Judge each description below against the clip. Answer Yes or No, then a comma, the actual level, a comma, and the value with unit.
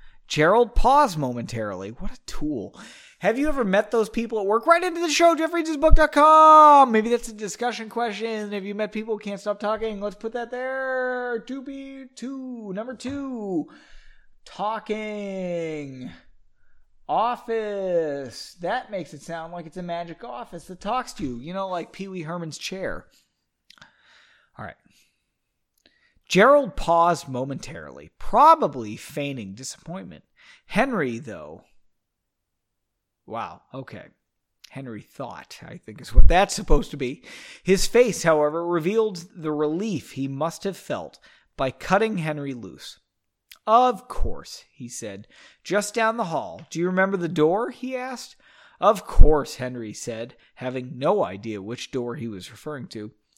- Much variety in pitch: Yes, wide, 7.4 semitones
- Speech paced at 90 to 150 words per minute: Yes, average, 140 wpm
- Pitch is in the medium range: No, high, 205 Hz